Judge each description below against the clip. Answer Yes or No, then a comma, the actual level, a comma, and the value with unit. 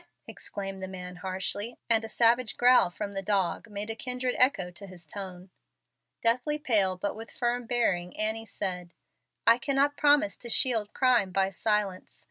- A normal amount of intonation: Yes, average, 4.3 semitones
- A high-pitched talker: Yes, high, 210 Hz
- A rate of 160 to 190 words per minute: Yes, average, 165 wpm